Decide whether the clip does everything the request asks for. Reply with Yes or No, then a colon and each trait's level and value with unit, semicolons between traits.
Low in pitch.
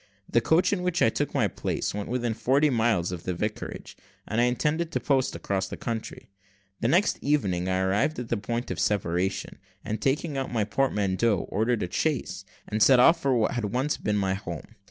Yes: low, 115 Hz